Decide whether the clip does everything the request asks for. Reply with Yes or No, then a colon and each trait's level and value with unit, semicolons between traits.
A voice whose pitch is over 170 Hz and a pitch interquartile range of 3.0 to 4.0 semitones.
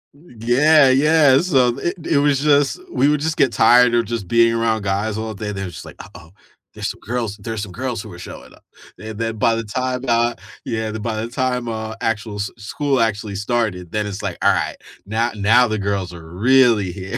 No: low, 115 Hz; average, 3.5 semitones